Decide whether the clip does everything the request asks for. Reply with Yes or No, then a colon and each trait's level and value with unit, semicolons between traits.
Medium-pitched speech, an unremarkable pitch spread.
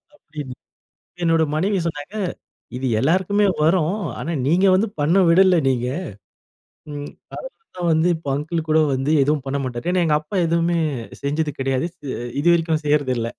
Yes: medium, 155 Hz; average, 3.1 semitones